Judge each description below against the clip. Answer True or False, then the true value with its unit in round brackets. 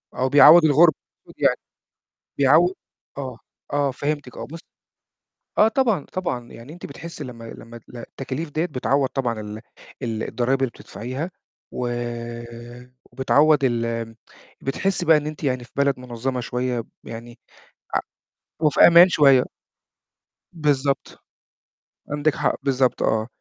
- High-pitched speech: False (135 Hz)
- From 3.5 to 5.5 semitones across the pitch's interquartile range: True (3.9 semitones)